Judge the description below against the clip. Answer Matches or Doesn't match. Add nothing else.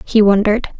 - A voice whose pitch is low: Doesn't match